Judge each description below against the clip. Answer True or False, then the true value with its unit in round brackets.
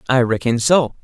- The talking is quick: False (175 wpm)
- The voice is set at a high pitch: False (125 Hz)